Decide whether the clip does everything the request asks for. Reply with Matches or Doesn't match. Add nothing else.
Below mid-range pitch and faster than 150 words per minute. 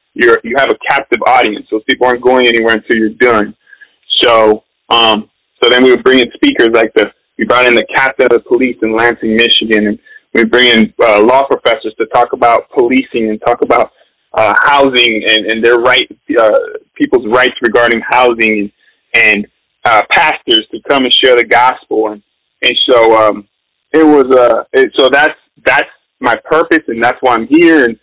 Matches